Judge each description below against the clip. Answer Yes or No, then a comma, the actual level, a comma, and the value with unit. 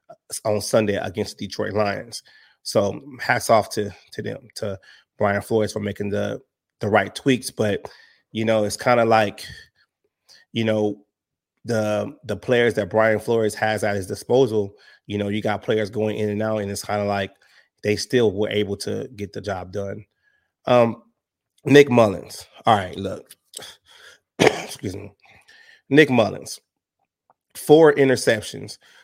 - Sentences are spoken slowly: No, average, 155 wpm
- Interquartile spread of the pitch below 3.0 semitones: Yes, narrow, 2.4 semitones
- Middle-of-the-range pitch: No, low, 110 Hz